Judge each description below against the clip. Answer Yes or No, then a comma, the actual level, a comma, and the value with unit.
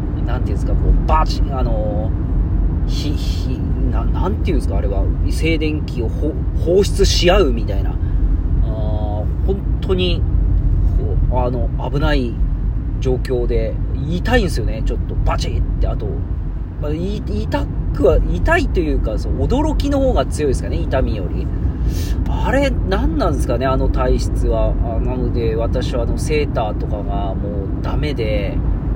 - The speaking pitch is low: Yes, very low, 85 Hz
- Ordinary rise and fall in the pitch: Yes, average, 3.0 semitones